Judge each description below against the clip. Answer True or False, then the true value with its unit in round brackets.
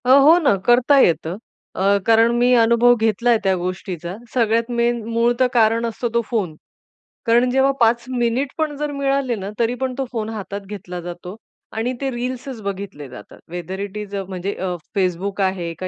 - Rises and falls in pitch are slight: False (4.2 semitones)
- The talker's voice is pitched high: True (225 Hz)